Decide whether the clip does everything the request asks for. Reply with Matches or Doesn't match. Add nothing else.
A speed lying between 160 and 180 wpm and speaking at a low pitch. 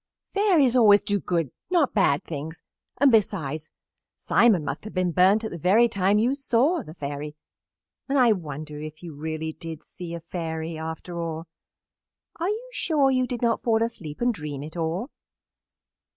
Doesn't match